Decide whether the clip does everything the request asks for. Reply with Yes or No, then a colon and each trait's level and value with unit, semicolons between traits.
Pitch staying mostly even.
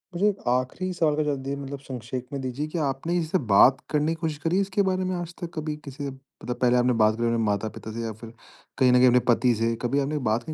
No: average, 4.4 semitones